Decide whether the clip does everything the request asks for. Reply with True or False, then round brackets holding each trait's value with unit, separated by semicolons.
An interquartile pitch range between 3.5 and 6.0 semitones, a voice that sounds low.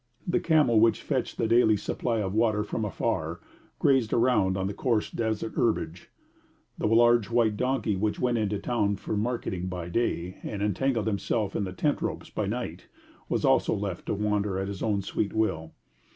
False (3.0 semitones; 105 Hz)